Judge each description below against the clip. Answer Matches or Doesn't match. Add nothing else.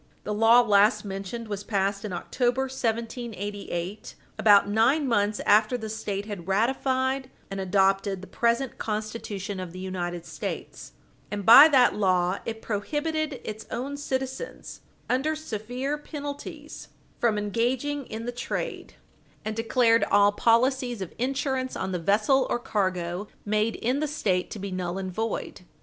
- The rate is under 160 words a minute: Matches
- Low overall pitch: Doesn't match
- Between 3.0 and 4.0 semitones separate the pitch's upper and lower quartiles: Doesn't match